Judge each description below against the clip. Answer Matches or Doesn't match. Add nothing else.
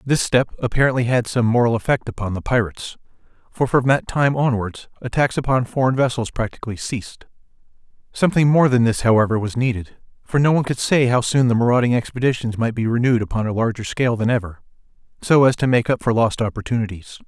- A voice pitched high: Doesn't match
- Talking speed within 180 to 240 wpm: Matches